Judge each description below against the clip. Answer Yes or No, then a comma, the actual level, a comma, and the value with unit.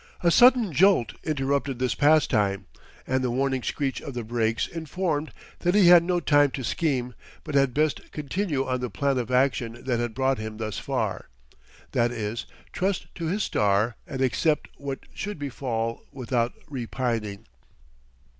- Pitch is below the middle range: Yes, low, 130 Hz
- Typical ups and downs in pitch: Yes, average, 4.4 semitones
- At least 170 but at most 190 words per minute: No, average, 160 wpm